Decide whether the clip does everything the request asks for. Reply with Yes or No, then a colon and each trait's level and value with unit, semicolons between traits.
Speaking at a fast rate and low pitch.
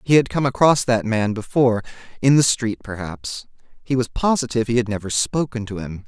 No: average, 190 wpm; low, 120 Hz